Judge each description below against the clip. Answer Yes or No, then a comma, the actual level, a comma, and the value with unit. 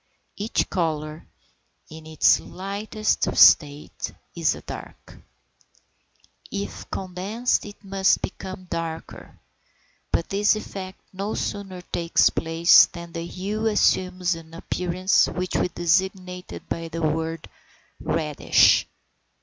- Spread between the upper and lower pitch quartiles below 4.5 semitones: Yes, average, 2.8 semitones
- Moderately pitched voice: Yes, medium, 180 Hz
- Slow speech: Yes, slow, 110 wpm